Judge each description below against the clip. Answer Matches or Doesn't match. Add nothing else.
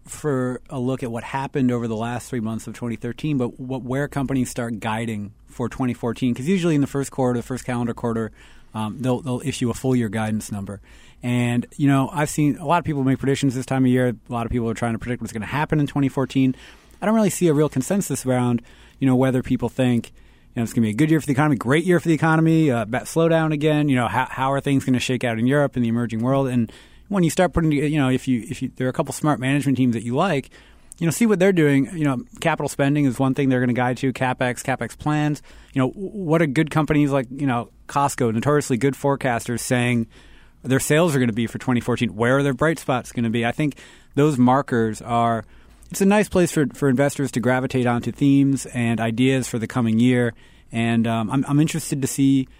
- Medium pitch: Doesn't match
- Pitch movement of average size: Matches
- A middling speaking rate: Doesn't match